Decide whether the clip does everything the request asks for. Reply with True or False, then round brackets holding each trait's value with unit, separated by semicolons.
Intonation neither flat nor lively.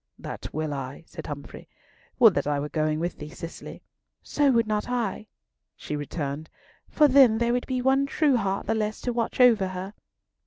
False (8.2 semitones)